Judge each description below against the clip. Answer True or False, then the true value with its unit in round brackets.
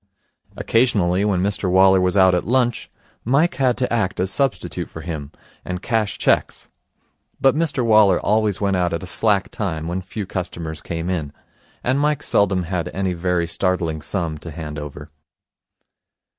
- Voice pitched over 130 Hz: False (95 Hz)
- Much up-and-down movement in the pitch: False (4.0 semitones)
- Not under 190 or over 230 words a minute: False (165 wpm)